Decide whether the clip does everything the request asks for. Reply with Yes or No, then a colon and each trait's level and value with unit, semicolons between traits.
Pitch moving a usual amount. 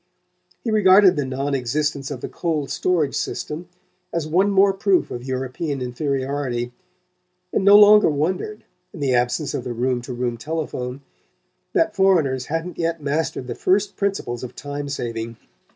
No: wide, 6.0 semitones